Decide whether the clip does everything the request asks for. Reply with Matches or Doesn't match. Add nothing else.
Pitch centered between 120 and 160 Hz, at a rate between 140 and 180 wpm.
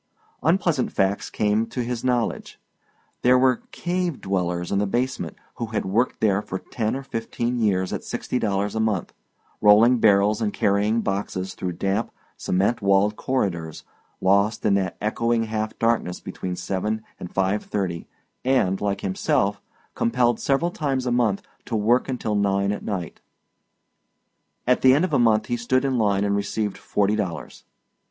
Doesn't match